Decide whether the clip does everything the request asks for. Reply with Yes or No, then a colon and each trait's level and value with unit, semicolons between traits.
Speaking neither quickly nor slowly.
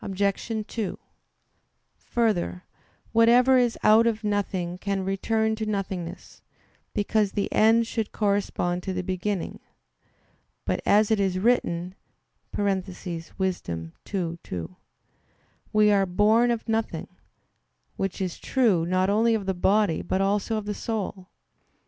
No: slow, 120 wpm